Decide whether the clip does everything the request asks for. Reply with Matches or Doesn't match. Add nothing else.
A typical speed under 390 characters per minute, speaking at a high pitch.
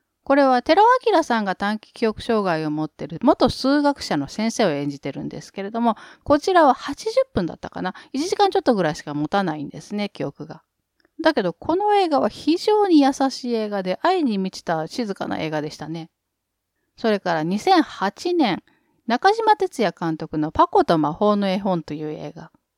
Matches